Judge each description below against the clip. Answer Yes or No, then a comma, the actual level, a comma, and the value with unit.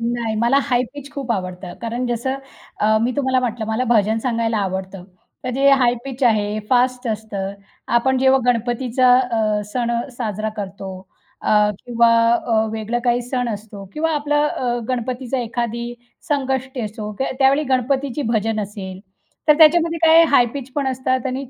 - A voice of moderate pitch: No, high, 240 Hz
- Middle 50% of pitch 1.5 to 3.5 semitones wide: Yes, average, 3.2 semitones